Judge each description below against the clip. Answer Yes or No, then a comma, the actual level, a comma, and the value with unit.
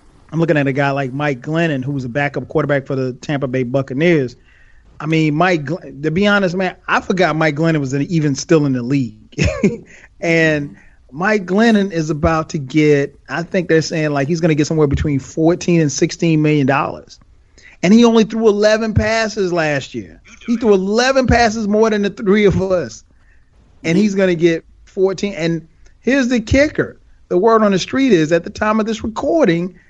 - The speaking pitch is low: No, medium, 165 Hz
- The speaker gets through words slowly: No, average, 195 wpm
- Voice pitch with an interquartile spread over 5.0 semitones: Yes, wide, 5.6 semitones